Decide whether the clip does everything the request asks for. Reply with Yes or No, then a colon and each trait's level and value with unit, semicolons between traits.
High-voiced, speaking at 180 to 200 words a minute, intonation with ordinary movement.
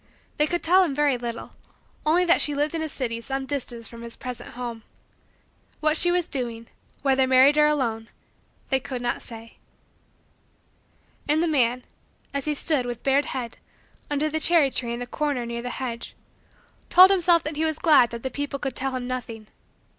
Yes: very high, 270 Hz; average, 190 wpm; average, 4.0 semitones